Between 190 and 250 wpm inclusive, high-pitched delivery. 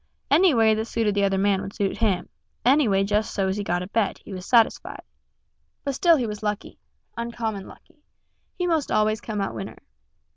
Yes: average, 195 wpm; high, 215 Hz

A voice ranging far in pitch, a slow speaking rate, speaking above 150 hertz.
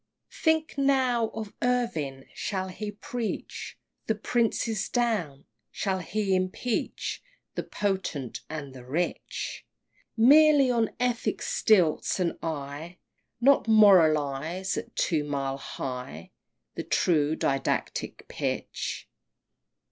Yes: wide, 7.6 semitones; slow, 105 wpm; high, 190 Hz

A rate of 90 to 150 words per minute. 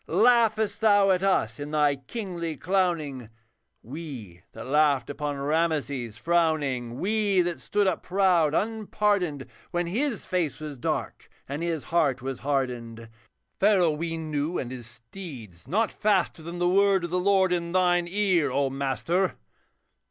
Yes: average, 145 wpm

